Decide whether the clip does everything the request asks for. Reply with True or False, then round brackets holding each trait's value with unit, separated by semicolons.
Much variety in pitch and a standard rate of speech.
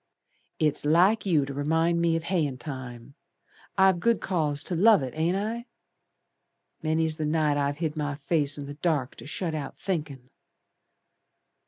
False (3.2 semitones; 160 wpm)